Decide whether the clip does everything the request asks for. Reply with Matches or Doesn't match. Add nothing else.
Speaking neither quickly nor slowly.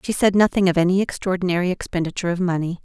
Matches